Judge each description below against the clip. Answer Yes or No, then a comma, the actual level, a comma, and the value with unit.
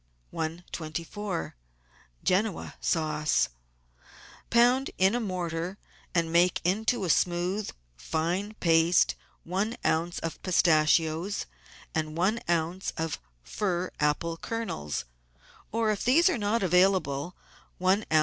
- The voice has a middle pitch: Yes, medium, 175 Hz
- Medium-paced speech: No, slow, 105 wpm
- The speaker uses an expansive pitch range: No, average, 4.0 semitones